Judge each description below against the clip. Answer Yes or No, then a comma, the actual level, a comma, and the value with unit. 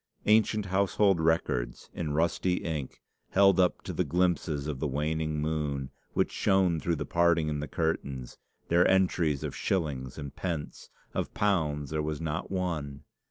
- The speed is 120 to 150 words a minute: No, average, 160 wpm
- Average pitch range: Yes, average, 3.5 semitones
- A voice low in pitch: Yes, very low, 80 Hz